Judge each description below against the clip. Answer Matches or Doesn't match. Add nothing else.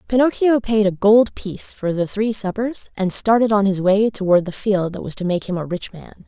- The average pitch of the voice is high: Matches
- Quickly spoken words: Matches